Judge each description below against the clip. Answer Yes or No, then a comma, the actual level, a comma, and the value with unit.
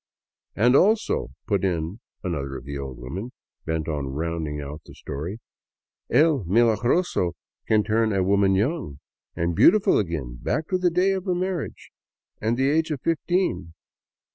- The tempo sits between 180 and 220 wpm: No, average, 165 wpm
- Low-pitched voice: Yes, low, 100 Hz